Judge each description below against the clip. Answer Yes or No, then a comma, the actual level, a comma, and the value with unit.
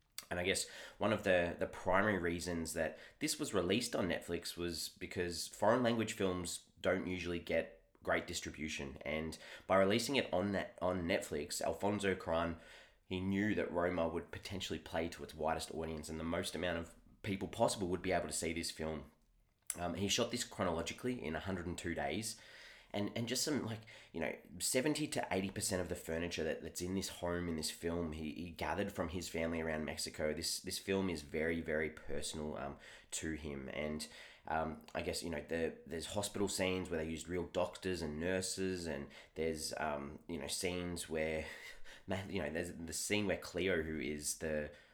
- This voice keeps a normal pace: Yes, average, 195 wpm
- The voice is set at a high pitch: No, very low, 85 Hz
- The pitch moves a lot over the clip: No, average, 2.9 semitones